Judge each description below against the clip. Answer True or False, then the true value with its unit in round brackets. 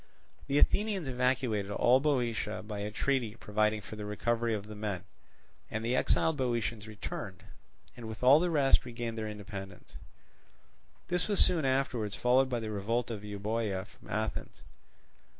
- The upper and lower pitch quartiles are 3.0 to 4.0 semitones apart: True (3.7 semitones)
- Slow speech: False (155 wpm)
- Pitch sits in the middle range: False (115 Hz)